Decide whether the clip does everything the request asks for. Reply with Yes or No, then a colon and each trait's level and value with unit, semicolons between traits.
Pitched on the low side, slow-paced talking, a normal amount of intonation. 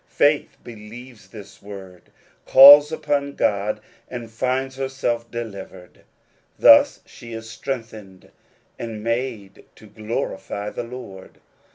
Yes: low, 115 Hz; slow, 105 wpm; average, 3.8 semitones